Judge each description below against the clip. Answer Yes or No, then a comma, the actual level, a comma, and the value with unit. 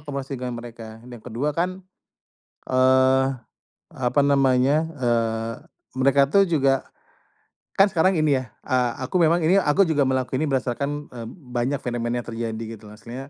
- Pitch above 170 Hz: No, low, 130 Hz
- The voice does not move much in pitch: No, average, 3.5 semitones